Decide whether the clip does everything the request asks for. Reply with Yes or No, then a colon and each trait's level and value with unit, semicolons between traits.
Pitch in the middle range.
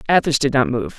Yes: medium, 145 Hz